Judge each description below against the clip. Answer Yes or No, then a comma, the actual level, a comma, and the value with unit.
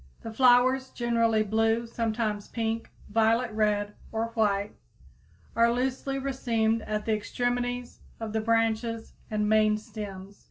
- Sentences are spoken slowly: Yes, slow, 125 wpm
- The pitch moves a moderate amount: No, narrow, 1.9 semitones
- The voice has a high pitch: Yes, high, 225 Hz